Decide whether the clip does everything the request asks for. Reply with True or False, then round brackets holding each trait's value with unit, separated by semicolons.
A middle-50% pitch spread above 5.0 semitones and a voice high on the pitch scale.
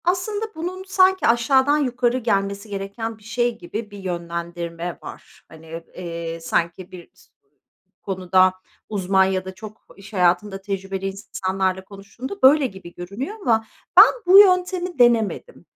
True (5.4 semitones; 200 Hz)